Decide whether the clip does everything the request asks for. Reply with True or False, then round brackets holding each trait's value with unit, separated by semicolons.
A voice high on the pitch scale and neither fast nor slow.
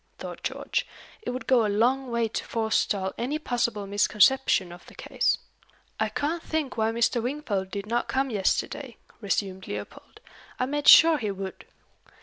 True (235 Hz; 160 wpm)